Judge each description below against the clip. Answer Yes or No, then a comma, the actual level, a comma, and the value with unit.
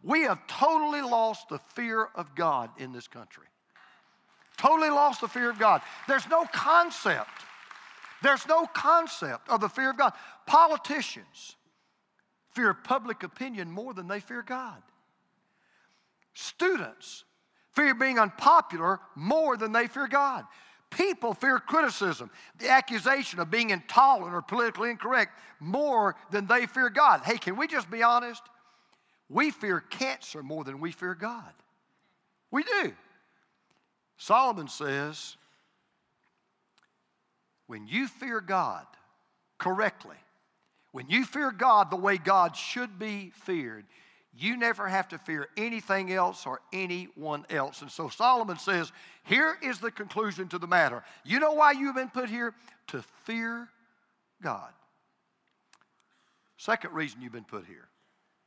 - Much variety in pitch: Yes, wide, 6.1 semitones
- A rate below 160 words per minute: Yes, slow, 135 wpm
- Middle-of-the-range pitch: No, high, 230 Hz